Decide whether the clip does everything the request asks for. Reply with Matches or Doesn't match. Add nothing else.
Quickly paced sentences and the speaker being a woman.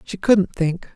Doesn't match